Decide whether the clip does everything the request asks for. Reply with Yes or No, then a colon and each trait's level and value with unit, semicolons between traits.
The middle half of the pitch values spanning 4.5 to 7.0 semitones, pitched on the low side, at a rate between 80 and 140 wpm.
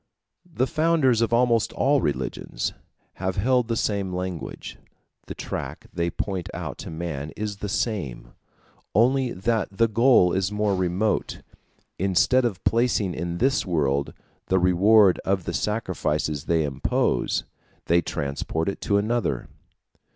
Yes: average, 5.0 semitones; very low, 95 Hz; slow, 135 wpm